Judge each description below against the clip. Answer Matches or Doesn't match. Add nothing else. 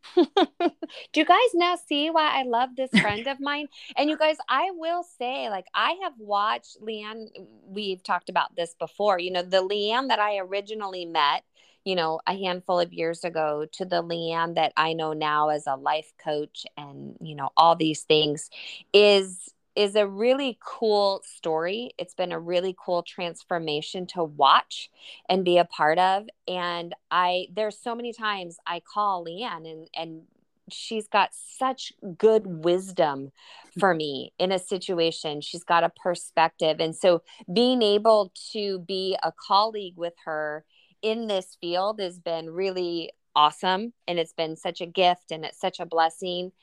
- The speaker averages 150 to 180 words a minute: Matches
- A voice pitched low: Doesn't match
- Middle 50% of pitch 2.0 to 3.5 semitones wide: Doesn't match